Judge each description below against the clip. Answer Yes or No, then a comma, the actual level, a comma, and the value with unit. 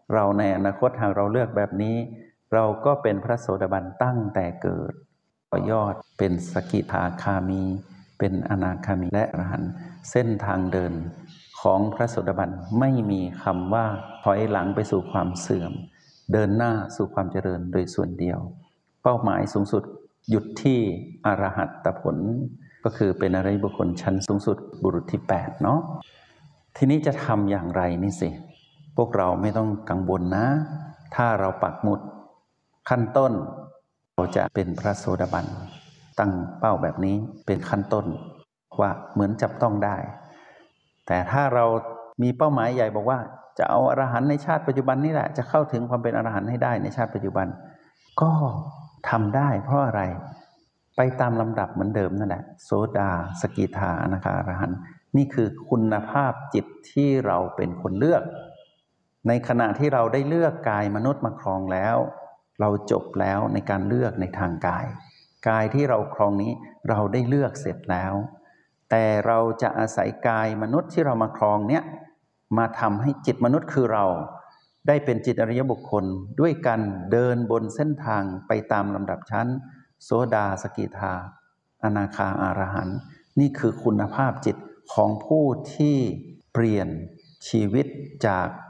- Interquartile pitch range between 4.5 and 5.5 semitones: Yes, average, 4.9 semitones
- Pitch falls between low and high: No, low, 110 Hz